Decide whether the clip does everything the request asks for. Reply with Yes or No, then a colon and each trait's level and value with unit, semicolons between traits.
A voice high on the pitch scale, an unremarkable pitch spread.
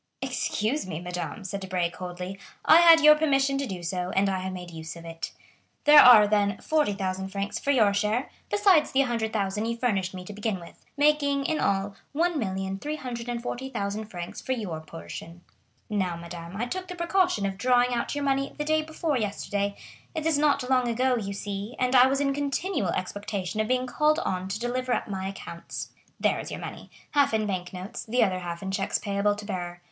No: high, 215 Hz; wide, 6.2 semitones